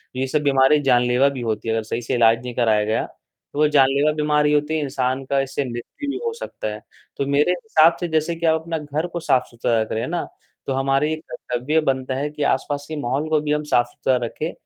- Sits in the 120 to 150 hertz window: Yes, medium, 140 Hz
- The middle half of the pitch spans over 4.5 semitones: No, average, 3.8 semitones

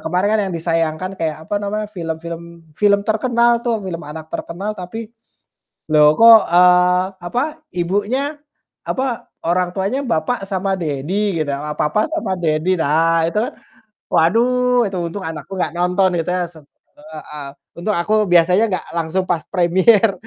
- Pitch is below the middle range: No, medium, 185 Hz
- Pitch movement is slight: No, average, 4.3 semitones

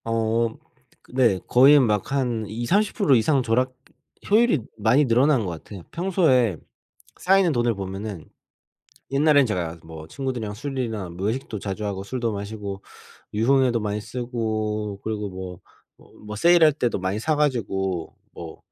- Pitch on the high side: No, low, 115 Hz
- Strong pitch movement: No, average, 4.9 semitones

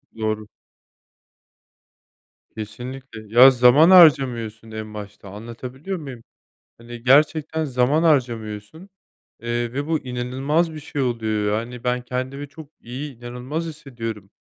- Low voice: Yes, low, 125 Hz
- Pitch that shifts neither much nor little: Yes, average, 4.1 semitones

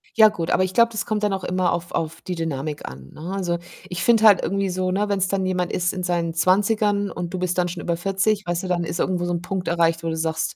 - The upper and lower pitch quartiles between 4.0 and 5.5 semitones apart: No, narrow, 2.5 semitones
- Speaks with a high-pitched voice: No, medium, 180 Hz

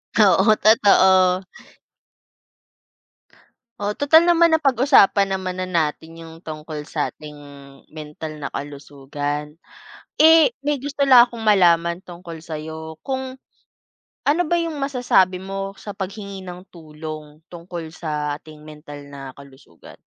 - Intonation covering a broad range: Yes, wide, 6.1 semitones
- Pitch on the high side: No, medium, 180 Hz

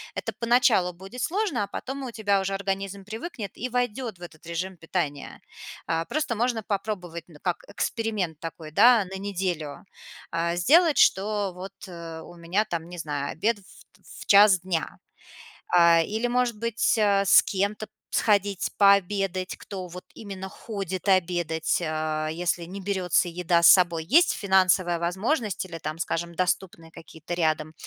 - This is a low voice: No, high, 190 Hz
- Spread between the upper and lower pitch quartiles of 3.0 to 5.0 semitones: Yes, average, 3.7 semitones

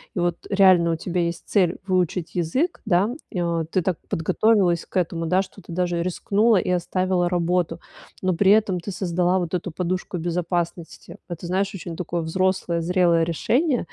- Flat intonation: Yes, narrow, 1.8 semitones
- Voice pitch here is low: No, medium, 180 Hz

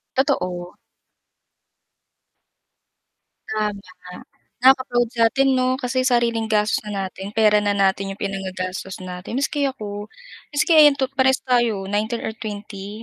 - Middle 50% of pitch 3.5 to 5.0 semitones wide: Yes, average, 4.4 semitones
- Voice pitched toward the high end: Yes, high, 215 Hz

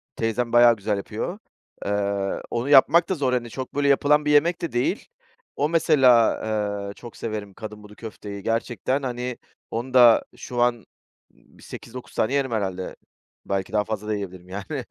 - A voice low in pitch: Yes, low, 115 Hz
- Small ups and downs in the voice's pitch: No, average, 4.1 semitones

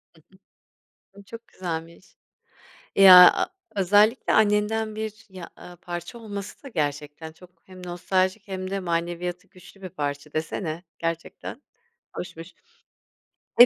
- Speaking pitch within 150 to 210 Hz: Yes, medium, 185 Hz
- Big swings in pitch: No, average, 3.4 semitones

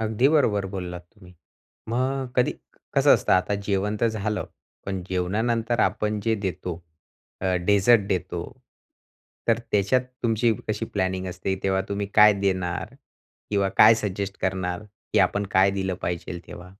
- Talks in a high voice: No, low, 100 Hz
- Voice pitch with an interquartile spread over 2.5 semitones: Yes, average, 2.9 semitones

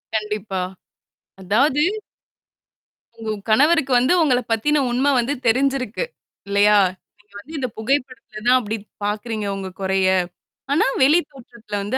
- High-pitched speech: Yes, high, 230 Hz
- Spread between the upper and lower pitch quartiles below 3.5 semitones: No, average, 4.5 semitones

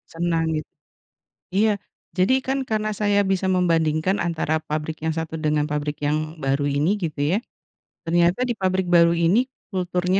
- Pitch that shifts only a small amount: No, average, 3.2 semitones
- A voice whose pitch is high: No, medium, 170 Hz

